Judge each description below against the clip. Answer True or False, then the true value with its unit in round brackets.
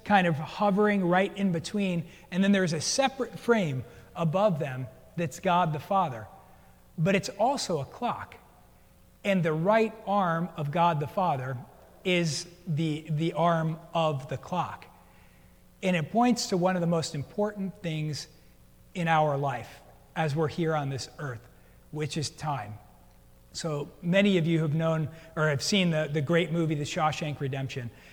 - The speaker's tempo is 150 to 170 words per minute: True (160 wpm)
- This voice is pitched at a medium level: True (160 Hz)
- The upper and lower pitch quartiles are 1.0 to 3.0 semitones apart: False (4.0 semitones)